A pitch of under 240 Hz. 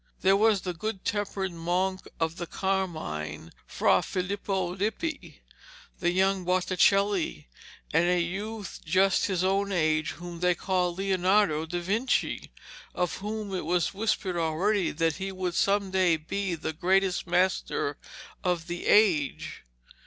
Yes: medium, 185 Hz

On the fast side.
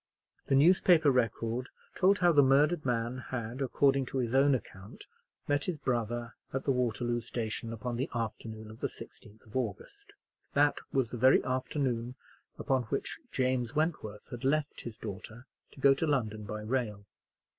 No: average, 165 wpm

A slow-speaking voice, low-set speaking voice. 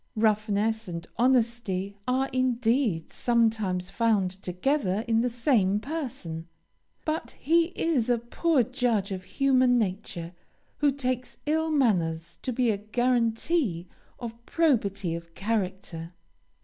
No: slow, 120 wpm; high, 225 Hz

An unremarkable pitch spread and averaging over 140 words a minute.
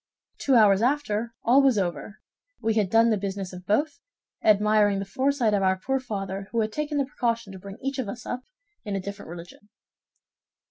Yes: average, 4.0 semitones; average, 195 wpm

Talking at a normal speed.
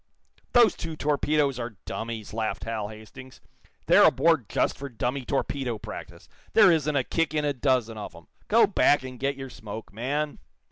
Yes: average, 175 wpm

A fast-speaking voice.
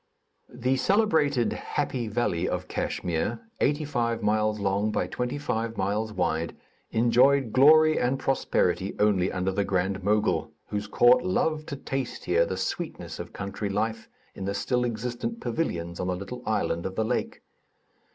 No: average, 155 wpm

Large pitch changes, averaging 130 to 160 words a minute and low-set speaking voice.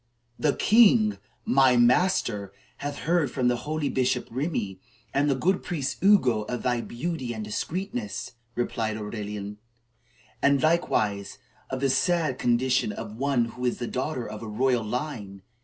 No: average, 5.0 semitones; average, 150 wpm; low, 125 Hz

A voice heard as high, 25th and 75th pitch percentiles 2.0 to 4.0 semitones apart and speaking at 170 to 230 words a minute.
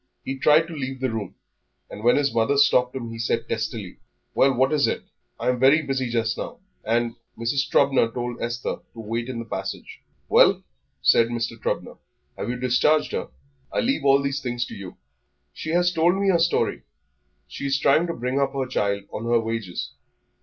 No: low, 125 Hz; average, 3.3 semitones; average, 200 wpm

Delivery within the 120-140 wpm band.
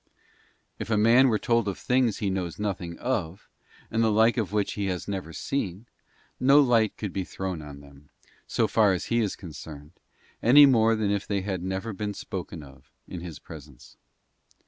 No: average, 190 wpm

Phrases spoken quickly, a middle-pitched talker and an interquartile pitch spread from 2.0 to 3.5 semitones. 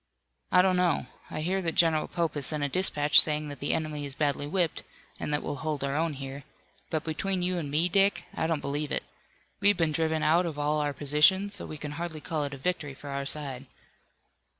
Yes: fast, 225 wpm; medium, 155 Hz; average, 2.9 semitones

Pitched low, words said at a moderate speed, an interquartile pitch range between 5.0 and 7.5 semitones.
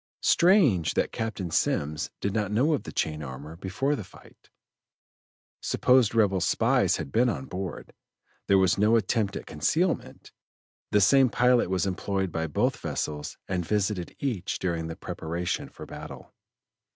Yes: very low, 95 Hz; average, 150 wpm; wide, 5.5 semitones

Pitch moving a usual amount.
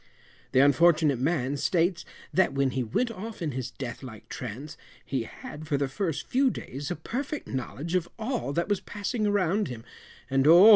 No: wide, 6.7 semitones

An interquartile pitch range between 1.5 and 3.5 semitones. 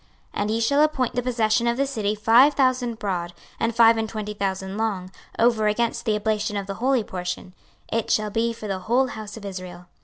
Yes: average, 2.7 semitones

